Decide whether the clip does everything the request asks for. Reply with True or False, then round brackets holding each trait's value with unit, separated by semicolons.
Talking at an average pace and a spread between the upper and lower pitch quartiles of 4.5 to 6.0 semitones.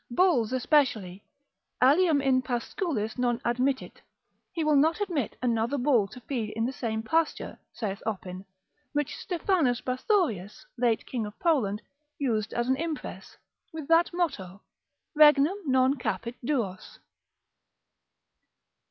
False (125 wpm; 5.4 semitones)